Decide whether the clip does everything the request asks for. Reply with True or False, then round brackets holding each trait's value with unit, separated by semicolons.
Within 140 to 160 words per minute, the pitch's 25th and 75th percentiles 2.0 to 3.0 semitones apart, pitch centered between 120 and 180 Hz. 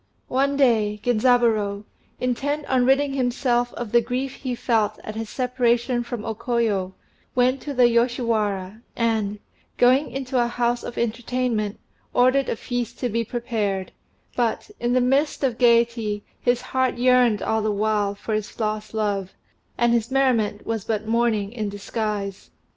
False (155 wpm; 2.7 semitones; 235 Hz)